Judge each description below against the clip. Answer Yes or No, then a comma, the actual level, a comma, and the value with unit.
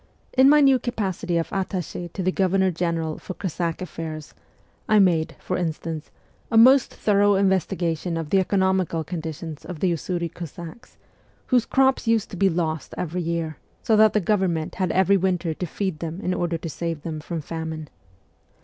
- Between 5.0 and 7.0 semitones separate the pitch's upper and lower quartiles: No, average, 3.0 semitones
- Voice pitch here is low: No, medium, 175 Hz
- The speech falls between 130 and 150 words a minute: No, average, 175 wpm